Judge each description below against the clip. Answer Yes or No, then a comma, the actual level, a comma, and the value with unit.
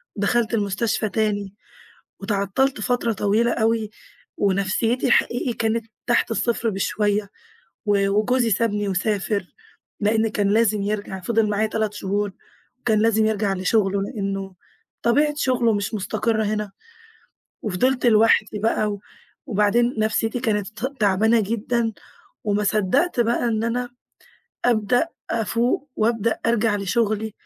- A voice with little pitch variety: Yes, narrow, 2.3 semitones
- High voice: Yes, high, 215 Hz